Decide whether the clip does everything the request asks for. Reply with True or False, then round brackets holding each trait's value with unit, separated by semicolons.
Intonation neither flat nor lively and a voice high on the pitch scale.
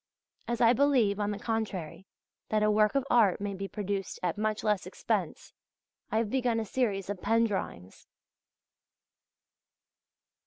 False (2.3 semitones; 210 Hz)